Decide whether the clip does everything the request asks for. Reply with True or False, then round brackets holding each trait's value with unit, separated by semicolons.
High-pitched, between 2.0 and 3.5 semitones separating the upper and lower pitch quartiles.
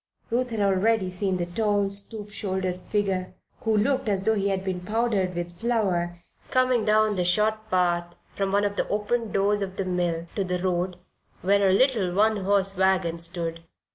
True (195 Hz; 2.8 semitones)